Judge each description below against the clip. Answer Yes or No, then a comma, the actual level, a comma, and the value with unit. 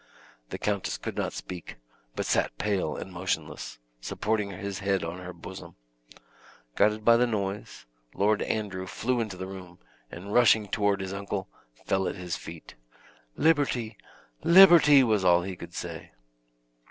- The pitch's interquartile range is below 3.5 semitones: Yes, average, 2.9 semitones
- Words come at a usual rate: Yes, average, 150 wpm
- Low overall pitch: Yes, low, 100 Hz